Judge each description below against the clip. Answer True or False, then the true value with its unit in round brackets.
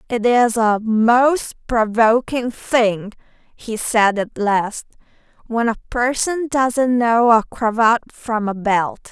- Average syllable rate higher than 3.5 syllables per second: False (3.2 syllables/s)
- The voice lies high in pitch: True (230 Hz)